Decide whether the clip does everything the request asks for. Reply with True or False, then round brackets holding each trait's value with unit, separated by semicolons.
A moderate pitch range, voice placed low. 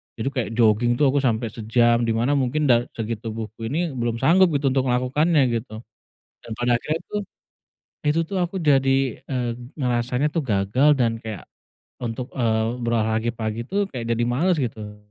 True (3.4 semitones; 120 Hz)